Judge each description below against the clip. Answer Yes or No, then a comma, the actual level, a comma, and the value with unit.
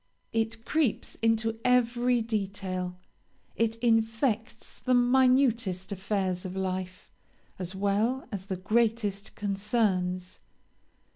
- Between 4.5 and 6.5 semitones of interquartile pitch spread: No, average, 3.6 semitones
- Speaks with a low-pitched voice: No, high, 220 Hz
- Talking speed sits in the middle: No, slow, 95 wpm